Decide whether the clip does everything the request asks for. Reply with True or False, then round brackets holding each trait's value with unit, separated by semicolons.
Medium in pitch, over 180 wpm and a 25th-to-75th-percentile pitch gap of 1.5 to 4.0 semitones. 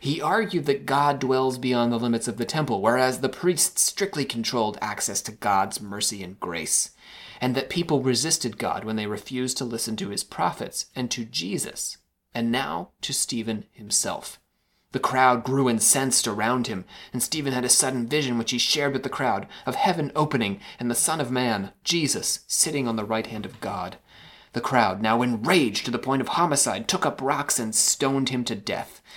False (125 Hz; 195 wpm; 3.0 semitones)